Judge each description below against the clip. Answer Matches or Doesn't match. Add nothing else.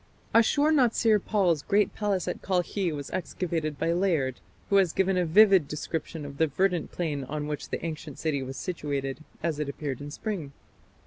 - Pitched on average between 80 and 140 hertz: Doesn't match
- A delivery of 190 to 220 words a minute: Doesn't match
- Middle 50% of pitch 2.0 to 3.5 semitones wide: Doesn't match